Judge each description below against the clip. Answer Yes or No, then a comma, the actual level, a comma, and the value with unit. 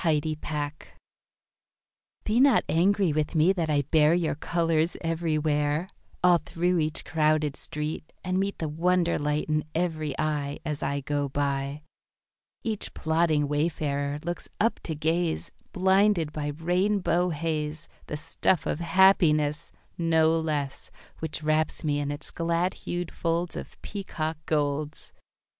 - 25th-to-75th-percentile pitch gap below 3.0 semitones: Yes, narrow, 2.5 semitones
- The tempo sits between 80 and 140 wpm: Yes, slow, 135 wpm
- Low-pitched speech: No, medium, 160 Hz